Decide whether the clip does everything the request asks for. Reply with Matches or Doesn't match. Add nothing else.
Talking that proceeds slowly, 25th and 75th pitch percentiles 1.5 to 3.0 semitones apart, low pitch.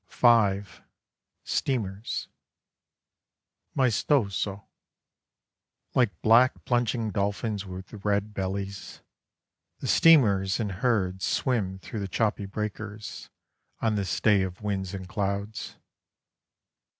Matches